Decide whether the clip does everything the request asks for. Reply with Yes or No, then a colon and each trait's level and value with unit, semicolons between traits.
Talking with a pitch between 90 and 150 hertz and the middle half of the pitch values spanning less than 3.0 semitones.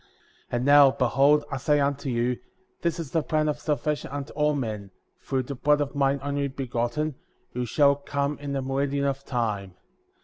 Yes: medium, 140 Hz; narrow, 2.4 semitones